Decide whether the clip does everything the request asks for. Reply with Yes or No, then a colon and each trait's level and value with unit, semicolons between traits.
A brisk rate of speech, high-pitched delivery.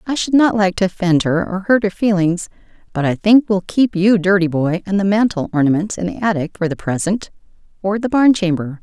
Yes: fast, 225 wpm; high, 195 Hz